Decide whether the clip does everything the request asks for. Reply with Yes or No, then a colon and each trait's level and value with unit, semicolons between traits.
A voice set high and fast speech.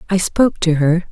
No: medium, 175 Hz; fast, 215 wpm